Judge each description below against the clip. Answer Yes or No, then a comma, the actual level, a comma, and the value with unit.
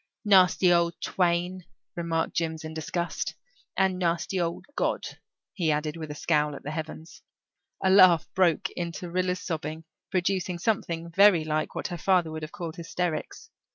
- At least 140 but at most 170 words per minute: Yes, average, 155 wpm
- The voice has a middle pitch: Yes, medium, 170 Hz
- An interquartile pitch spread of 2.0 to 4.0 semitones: Yes, narrow, 2.4 semitones